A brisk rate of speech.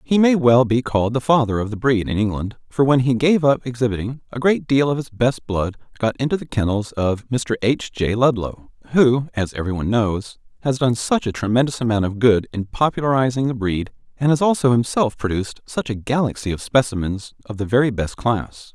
Yes: fast, 210 wpm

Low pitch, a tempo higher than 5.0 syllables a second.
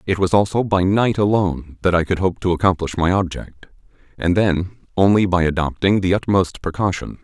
Yes: very low, 95 Hz; 5.4 syllables/s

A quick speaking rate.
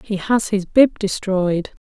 No: average, 165 wpm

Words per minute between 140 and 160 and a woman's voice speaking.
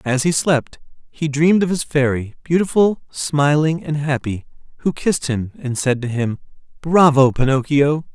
No: average, 155 wpm; male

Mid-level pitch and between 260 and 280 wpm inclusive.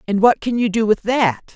No: high, 215 Hz; fast, 270 wpm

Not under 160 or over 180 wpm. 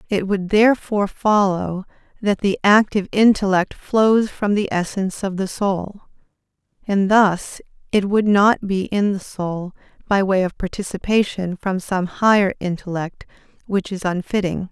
No: average, 145 wpm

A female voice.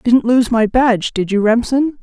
Yes: female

